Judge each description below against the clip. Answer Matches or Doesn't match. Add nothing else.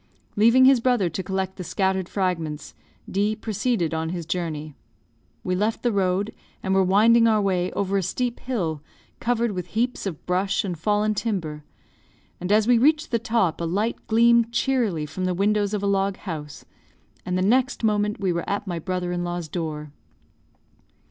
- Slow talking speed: Doesn't match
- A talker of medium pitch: Doesn't match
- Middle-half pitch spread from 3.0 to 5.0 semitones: Matches